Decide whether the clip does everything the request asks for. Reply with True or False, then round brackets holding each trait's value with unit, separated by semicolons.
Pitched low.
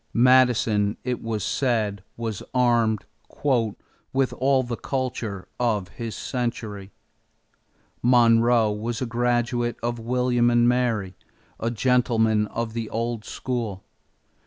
True (115 Hz)